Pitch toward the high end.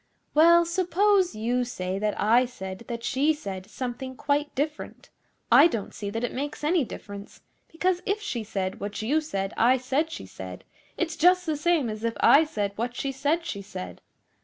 Yes: very high, 260 Hz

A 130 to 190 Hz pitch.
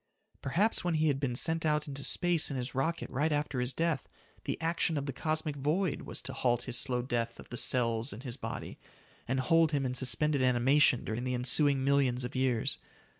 Yes: low, 135 Hz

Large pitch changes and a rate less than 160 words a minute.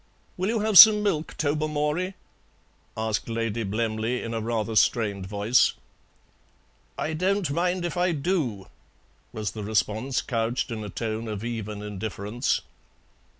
Yes: wide, 6.7 semitones; slow, 135 wpm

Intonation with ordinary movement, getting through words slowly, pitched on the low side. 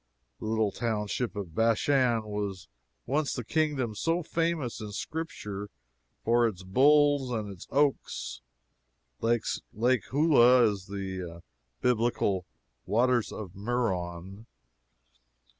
Yes: average, 4.3 semitones; slow, 105 wpm; low, 115 Hz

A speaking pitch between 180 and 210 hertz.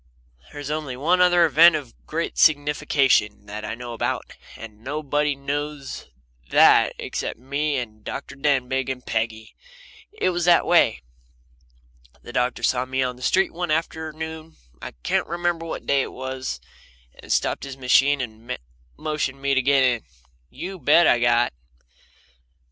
No: medium, 140 Hz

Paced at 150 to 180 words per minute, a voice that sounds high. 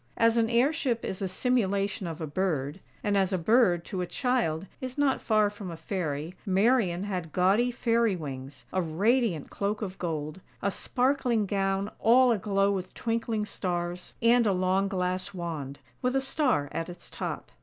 Yes: average, 175 wpm; high, 195 Hz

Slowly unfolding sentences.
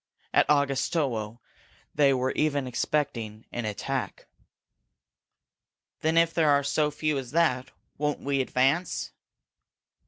Yes: slow, 115 wpm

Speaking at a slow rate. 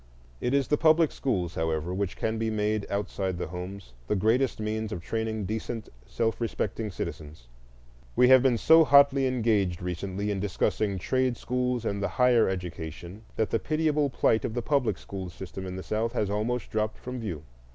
No: average, 185 wpm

